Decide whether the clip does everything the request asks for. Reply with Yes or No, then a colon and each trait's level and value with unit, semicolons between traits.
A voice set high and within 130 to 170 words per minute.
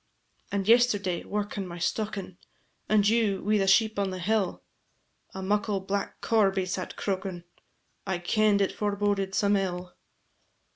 Yes: high, 200 Hz; average, 140 wpm